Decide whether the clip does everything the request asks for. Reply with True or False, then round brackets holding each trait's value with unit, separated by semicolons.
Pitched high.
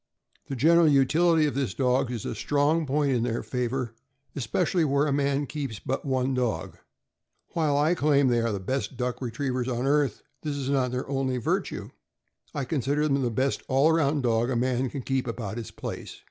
False (135 Hz)